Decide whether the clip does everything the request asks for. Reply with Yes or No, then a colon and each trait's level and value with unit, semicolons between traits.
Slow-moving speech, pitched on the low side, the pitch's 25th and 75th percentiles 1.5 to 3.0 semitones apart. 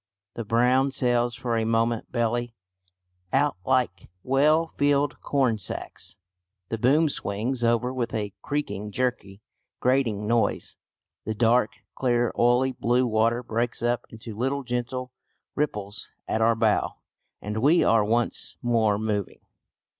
Yes: slow, 130 wpm; low, 120 Hz; narrow, 2.5 semitones